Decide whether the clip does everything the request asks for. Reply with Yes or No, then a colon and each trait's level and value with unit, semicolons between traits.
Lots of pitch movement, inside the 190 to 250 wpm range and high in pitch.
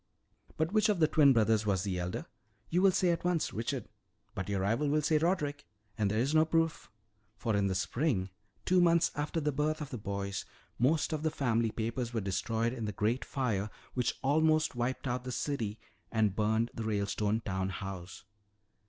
No: wide, 6.7 semitones; average, 195 wpm; low, 120 Hz